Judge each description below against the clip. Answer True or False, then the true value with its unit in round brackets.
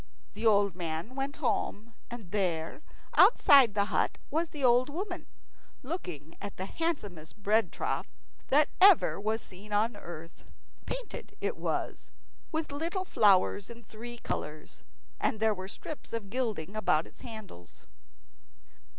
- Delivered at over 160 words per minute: False (140 wpm)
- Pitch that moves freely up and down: True (6.0 semitones)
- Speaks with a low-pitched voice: False (220 Hz)